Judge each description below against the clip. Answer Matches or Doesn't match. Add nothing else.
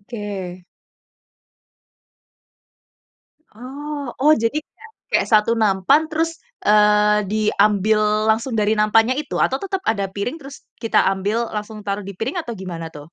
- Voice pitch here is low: Doesn't match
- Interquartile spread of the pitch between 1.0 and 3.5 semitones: Doesn't match